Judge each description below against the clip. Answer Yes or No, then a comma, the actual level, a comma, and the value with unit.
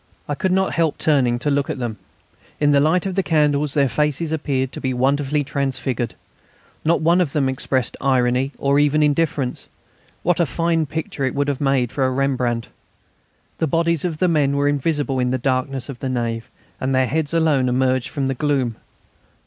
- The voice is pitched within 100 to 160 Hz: Yes, medium, 140 Hz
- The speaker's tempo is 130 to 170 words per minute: No, average, 195 wpm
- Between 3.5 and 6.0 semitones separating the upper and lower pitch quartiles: No, average, 2.8 semitones